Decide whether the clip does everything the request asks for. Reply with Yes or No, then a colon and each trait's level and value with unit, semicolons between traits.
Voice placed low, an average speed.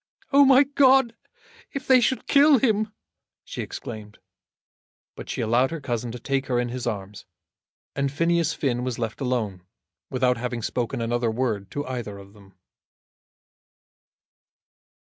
Yes: low, 125 Hz; average, 145 wpm